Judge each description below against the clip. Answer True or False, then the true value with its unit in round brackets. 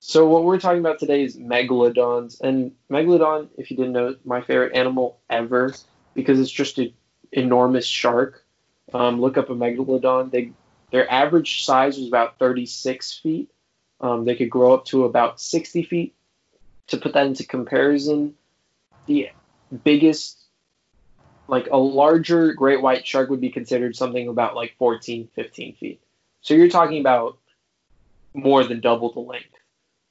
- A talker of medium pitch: False (130 Hz)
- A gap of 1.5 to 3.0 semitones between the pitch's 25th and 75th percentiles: True (2.7 semitones)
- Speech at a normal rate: True (155 wpm)